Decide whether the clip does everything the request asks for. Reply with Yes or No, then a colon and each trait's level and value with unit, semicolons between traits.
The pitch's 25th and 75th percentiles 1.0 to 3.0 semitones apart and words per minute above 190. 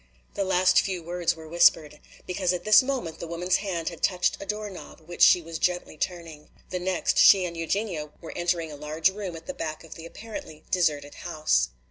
Yes: narrow, 2.4 semitones; fast, 205 wpm